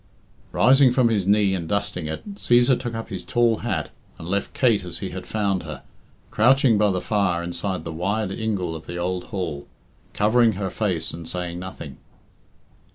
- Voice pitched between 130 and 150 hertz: No, low, 100 Hz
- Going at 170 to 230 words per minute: Yes, average, 180 wpm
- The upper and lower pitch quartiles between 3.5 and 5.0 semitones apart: Yes, average, 4.2 semitones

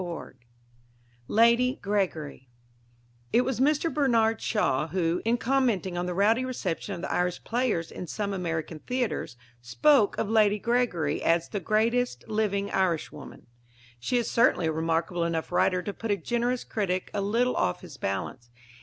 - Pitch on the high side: Yes, high, 200 Hz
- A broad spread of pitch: Yes, wide, 5.8 semitones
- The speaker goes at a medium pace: Yes, average, 155 wpm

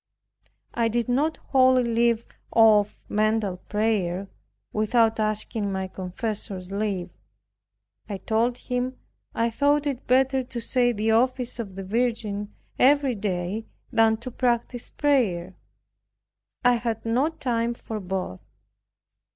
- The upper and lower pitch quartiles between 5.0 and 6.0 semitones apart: No, average, 3.2 semitones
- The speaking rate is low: Yes, slow, 120 wpm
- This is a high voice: Yes, high, 225 Hz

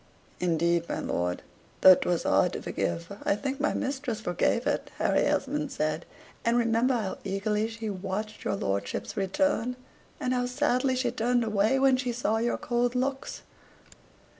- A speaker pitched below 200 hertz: No, high, 230 Hz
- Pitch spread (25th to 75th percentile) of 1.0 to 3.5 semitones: No, average, 4.5 semitones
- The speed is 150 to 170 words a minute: Yes, average, 160 wpm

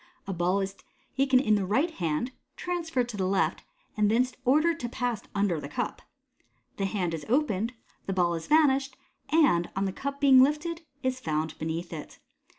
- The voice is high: Yes, high, 220 Hz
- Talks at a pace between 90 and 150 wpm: No, average, 180 wpm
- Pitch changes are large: Yes, wide, 7.1 semitones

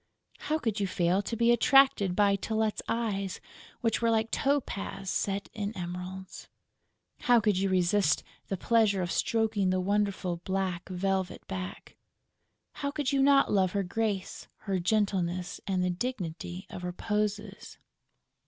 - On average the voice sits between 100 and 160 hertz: No, high, 200 Hz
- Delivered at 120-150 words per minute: Yes, average, 145 wpm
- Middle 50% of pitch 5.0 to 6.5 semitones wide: No, average, 3.2 semitones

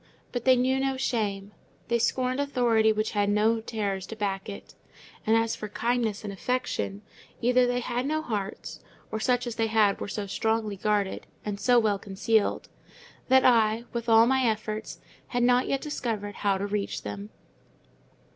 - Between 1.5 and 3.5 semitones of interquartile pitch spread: Yes, average, 3.1 semitones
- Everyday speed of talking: Yes, average, 175 wpm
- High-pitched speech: Yes, high, 225 Hz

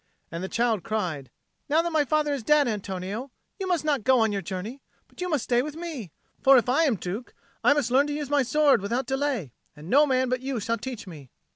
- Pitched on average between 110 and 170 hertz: No, very high, 255 Hz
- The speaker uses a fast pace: Yes, fast, 240 wpm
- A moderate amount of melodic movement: No, wide, 5.7 semitones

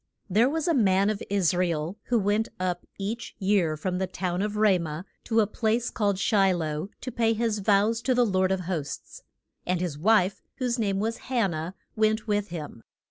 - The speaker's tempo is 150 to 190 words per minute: No, fast, 205 wpm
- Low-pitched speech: No, high, 200 Hz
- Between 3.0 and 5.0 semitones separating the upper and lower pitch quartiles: Yes, average, 3.6 semitones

